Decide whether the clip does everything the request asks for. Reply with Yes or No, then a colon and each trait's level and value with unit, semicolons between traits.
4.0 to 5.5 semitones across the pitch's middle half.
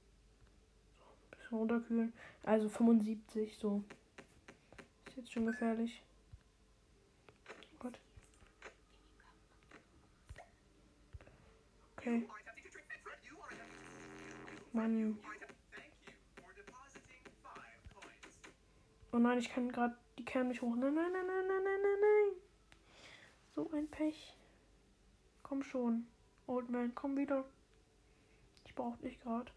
No: average, 3.6 semitones